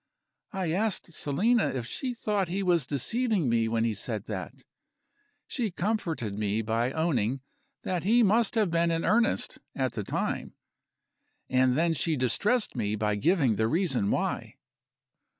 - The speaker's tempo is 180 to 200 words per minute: No, average, 150 wpm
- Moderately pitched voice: Yes, medium, 165 Hz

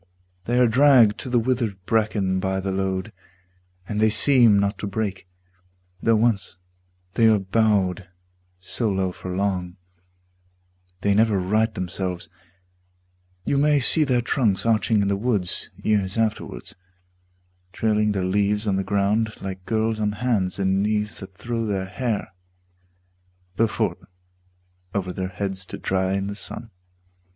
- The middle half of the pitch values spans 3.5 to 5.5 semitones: No, average, 2.8 semitones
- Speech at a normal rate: Yes, average, 145 wpm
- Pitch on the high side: No, low, 105 Hz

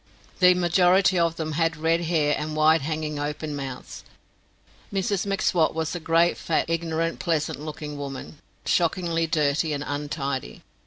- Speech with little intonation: Yes, narrow, 2.3 semitones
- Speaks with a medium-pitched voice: Yes, medium, 160 Hz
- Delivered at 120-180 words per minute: Yes, average, 145 wpm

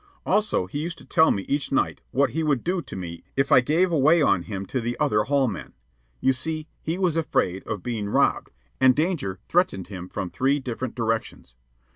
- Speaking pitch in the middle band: No, low, 130 Hz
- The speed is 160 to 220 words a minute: Yes, fast, 205 wpm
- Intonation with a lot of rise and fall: Yes, wide, 7.5 semitones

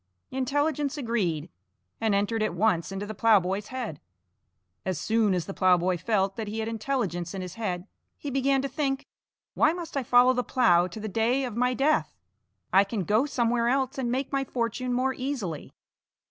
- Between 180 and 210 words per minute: Yes, average, 185 wpm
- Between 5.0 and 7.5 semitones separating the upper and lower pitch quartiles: Yes, average, 5.3 semitones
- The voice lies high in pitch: Yes, high, 230 Hz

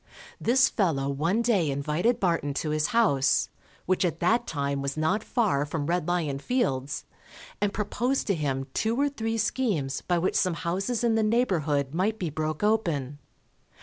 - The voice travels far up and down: Yes, wide, 7.4 semitones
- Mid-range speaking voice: Yes, medium, 175 Hz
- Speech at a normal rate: Yes, average, 170 wpm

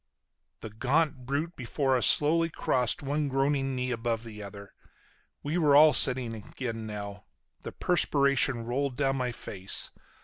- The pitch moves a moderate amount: Yes, average, 3.8 semitones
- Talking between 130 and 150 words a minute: Yes, average, 145 wpm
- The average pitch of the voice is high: No, low, 130 Hz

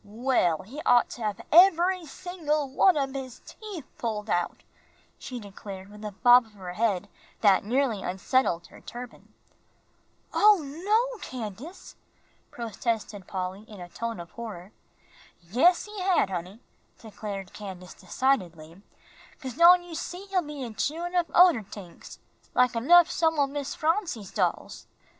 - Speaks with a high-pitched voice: Yes, high, 240 Hz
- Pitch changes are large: Yes, wide, 8.3 semitones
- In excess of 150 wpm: No, average, 145 wpm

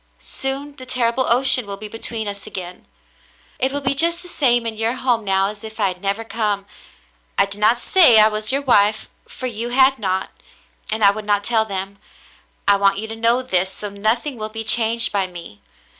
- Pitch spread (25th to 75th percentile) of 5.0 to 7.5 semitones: No, average, 3.5 semitones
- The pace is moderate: No, fast, 220 wpm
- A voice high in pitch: Yes, high, 220 Hz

